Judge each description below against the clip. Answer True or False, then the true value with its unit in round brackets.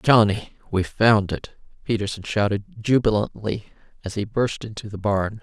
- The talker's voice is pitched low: True (105 Hz)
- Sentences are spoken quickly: False (145 wpm)